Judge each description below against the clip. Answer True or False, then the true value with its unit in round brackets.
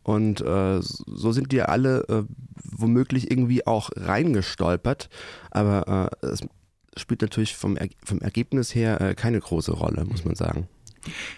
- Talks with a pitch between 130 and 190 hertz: False (110 Hz)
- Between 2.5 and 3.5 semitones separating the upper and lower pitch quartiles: False (4.3 semitones)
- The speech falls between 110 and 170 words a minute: True (155 wpm)